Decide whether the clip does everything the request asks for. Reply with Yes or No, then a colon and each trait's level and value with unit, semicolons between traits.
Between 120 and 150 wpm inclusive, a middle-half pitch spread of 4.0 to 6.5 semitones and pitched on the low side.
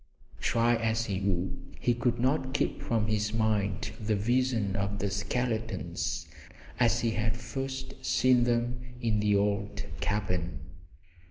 No: average, 140 wpm; average, 2.9 semitones; low, 110 Hz